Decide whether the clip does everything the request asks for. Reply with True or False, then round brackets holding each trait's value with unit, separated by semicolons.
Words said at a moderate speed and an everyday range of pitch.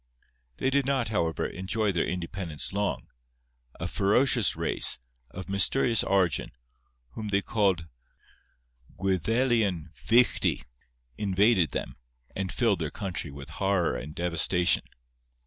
False (115 wpm; 4.3 semitones)